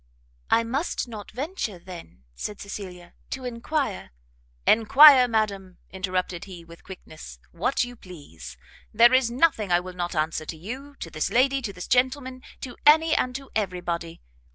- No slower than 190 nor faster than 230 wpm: No, average, 165 wpm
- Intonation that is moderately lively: No, wide, 6.4 semitones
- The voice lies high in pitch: Yes, high, 210 Hz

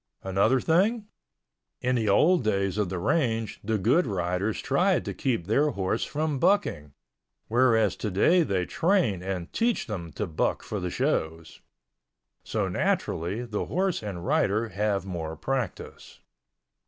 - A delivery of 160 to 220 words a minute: No, average, 140 wpm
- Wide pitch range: Yes, wide, 6.6 semitones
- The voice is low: Yes, low, 110 Hz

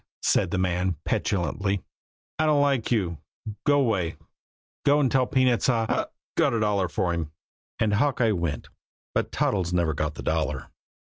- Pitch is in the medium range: No, low, 100 Hz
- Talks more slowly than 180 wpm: Yes, average, 160 wpm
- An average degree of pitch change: No, wide, 6.5 semitones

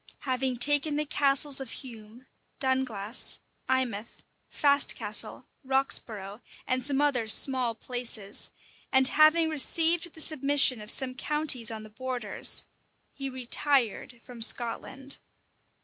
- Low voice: No, very high, 260 Hz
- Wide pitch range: No, average, 3.3 semitones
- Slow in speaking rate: Yes, slow, 115 wpm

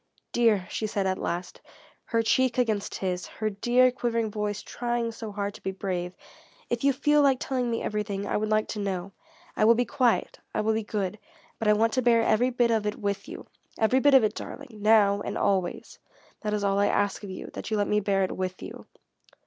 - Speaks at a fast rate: Yes, fast, 220 wpm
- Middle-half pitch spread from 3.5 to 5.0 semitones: No, average, 2.8 semitones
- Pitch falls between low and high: No, high, 215 Hz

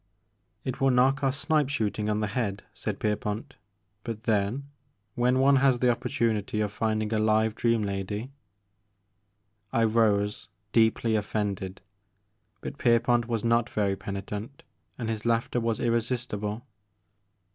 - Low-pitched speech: Yes, low, 110 Hz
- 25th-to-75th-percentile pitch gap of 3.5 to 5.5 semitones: No, average, 2.7 semitones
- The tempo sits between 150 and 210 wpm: No, average, 140 wpm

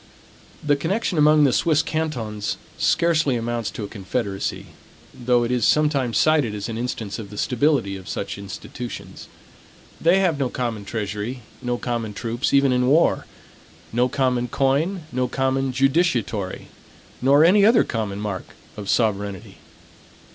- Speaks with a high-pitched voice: No, low, 125 Hz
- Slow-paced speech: No, average, 145 wpm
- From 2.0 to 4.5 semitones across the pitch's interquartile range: No, average, 5.1 semitones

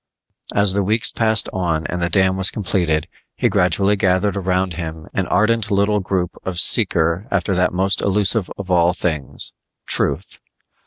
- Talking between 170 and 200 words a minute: No, average, 160 wpm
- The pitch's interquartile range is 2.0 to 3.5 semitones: Yes, narrow, 2.4 semitones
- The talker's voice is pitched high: No, very low, 95 Hz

